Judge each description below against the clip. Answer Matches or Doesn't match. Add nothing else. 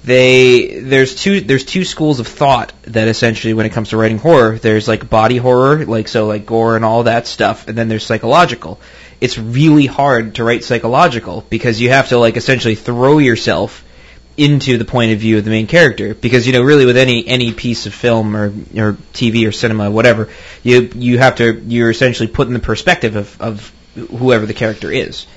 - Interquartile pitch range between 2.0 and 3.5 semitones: Matches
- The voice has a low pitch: Matches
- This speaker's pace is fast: Matches